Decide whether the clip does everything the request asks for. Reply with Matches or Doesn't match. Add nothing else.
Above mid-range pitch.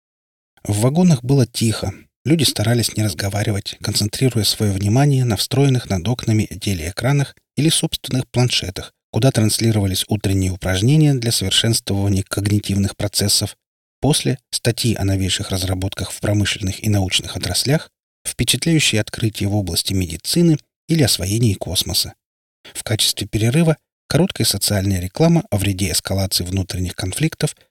Doesn't match